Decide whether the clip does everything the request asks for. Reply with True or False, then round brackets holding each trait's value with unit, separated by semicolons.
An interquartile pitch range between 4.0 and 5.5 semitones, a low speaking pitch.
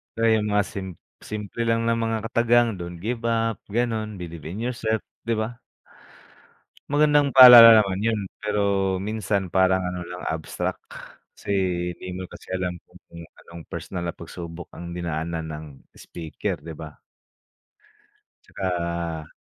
True (4.7 semitones; 95 Hz)